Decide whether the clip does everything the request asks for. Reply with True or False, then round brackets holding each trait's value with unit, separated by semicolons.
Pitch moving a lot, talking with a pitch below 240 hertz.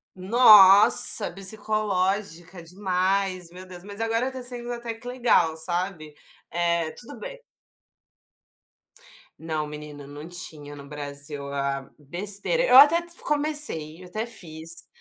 True (6.1 semitones; 185 Hz)